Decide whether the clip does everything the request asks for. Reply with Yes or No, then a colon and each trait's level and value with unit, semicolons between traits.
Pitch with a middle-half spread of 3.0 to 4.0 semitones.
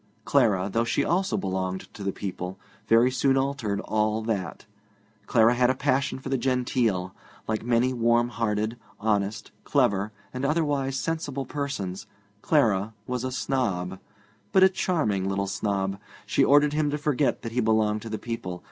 No: average, 4.8 semitones